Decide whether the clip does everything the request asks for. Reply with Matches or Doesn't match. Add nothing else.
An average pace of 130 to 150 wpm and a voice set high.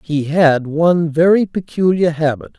Doesn't match